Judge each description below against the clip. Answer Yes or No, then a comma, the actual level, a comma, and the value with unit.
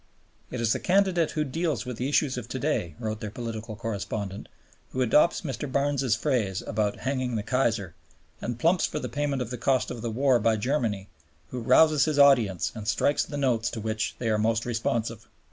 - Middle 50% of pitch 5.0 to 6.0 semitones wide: No, average, 4.2 semitones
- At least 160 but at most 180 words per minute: No, average, 200 wpm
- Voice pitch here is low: Yes, low, 120 Hz